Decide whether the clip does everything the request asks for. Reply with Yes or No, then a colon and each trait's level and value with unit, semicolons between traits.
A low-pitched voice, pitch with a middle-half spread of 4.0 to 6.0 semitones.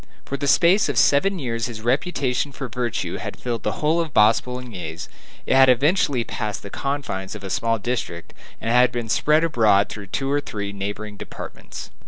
Yes: low, 120 Hz; average, 4.9 semitones